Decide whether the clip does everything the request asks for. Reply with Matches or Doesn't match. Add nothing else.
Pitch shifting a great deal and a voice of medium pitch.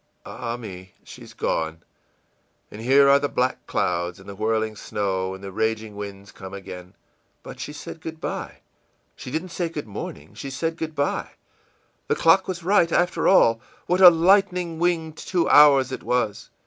Doesn't match